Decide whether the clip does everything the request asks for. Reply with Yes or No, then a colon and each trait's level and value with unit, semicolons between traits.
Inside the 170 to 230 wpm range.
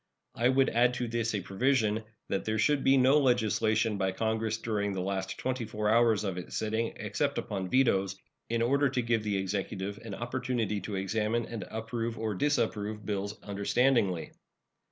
Yes: average, 175 wpm